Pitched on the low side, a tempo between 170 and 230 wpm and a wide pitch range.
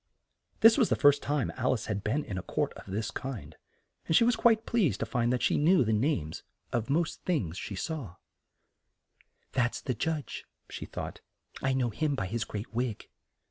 Yes: low, 130 Hz; average, 200 wpm; wide, 6.3 semitones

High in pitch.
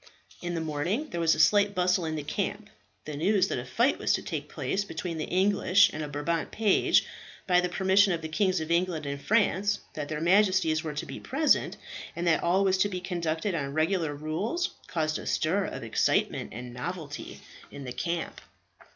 No: medium, 170 Hz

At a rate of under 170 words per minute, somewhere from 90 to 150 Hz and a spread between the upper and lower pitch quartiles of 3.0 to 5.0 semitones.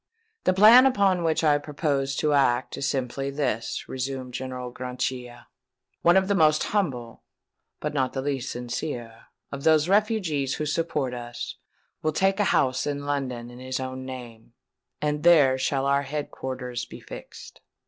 Yes: average, 160 wpm; low, 135 Hz; average, 3.4 semitones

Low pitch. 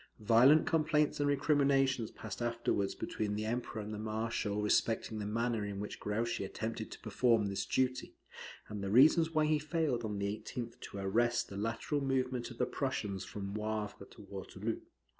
Yes: low, 115 Hz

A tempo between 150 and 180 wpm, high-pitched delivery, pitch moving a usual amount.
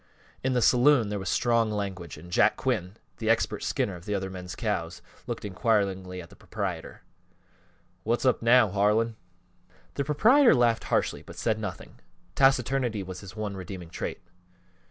No: average, 155 wpm; low, 105 Hz; average, 4.3 semitones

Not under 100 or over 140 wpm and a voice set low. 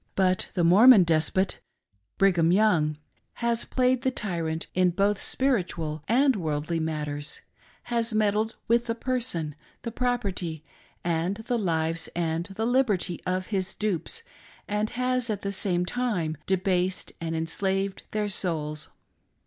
No: slow, 135 wpm; high, 190 Hz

